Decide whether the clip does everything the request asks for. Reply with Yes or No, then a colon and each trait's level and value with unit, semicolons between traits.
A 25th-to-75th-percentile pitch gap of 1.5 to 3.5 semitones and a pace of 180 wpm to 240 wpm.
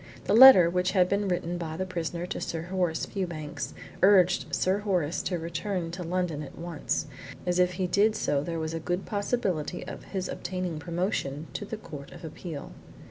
Yes: narrow, 2.4 semitones; average, 190 wpm